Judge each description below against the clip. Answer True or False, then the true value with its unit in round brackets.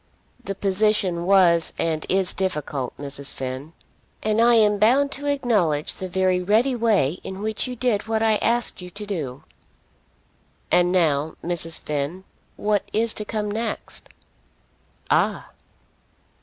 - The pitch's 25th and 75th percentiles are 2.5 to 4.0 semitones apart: False (4.7 semitones)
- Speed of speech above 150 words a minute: False (140 wpm)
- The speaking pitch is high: True (195 Hz)